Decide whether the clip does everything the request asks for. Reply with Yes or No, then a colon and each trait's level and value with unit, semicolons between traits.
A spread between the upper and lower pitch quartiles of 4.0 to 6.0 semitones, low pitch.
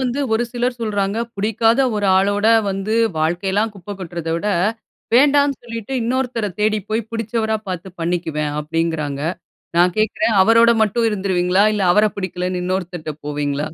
No: average, 4.3 semitones; high, 200 Hz